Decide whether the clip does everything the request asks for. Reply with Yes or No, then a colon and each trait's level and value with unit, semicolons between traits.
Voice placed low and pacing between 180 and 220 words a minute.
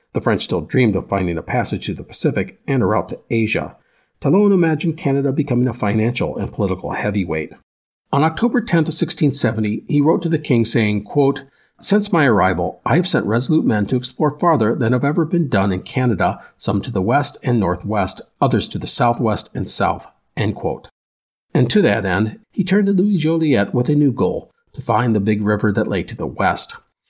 Yes: low, 125 Hz; average, 200 wpm